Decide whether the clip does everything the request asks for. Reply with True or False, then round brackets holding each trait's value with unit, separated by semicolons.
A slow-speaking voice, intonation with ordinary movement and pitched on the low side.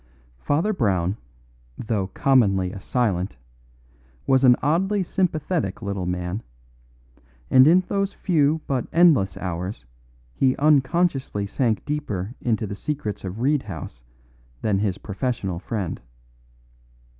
False (115 wpm; 7.4 semitones; 115 Hz)